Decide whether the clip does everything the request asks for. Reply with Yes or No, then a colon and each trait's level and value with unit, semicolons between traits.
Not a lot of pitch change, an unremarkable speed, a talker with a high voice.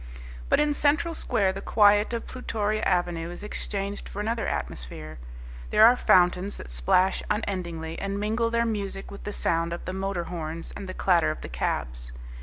No: average, 3.9 semitones; average, 180 wpm; high, 195 Hz